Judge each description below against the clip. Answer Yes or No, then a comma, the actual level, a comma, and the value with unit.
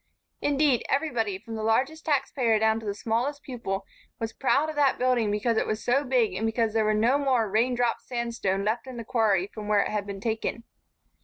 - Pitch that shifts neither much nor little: Yes, average, 3.2 semitones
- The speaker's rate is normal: No, fast, 220 wpm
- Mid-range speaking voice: No, high, 230 Hz